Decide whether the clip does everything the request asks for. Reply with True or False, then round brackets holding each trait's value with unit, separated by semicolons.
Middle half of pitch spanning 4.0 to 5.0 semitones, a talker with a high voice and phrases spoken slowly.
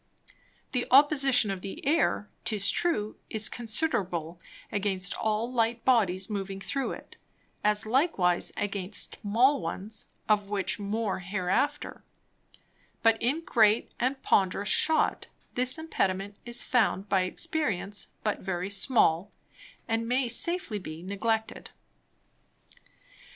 True (4.3 semitones; 215 Hz; 115 wpm)